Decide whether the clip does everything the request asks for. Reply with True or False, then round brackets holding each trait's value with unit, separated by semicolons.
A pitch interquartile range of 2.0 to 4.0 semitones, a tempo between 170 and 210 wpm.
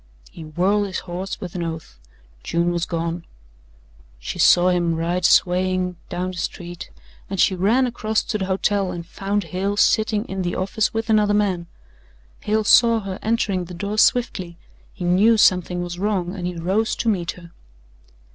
True (2.9 semitones; 175 wpm)